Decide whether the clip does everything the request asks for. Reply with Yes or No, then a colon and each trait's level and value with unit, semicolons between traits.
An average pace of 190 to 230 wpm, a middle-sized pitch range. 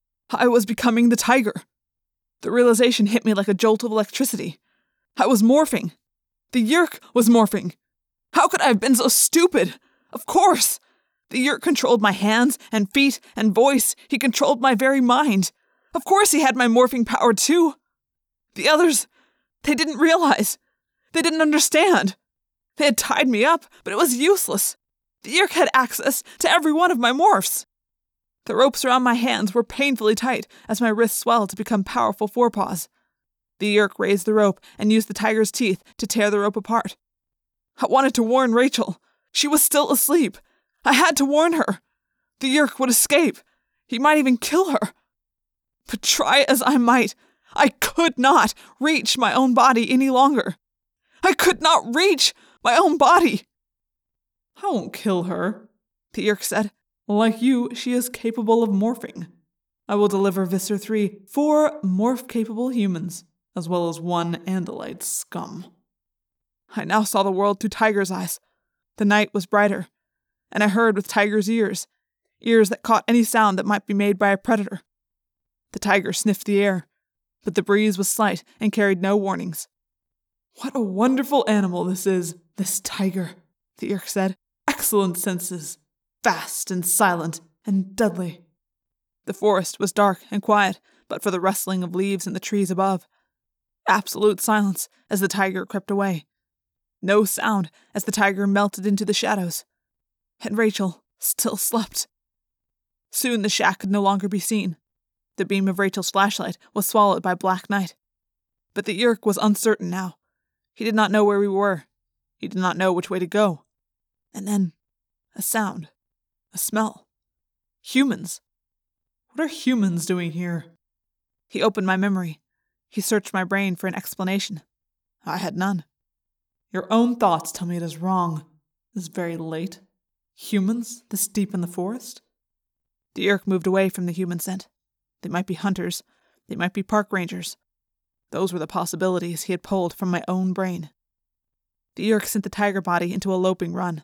No: average, 165 wpm; average, 4.5 semitones